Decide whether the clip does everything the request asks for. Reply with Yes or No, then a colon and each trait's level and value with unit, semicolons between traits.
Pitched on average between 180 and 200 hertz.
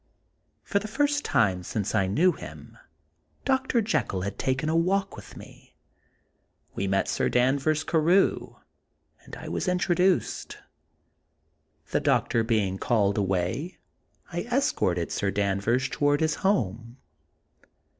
No: low, 135 Hz